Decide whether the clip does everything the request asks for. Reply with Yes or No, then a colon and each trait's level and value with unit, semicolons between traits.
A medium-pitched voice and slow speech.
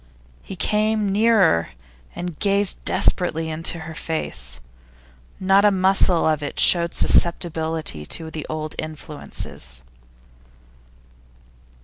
Yes: medium, 165 Hz; slow, 100 wpm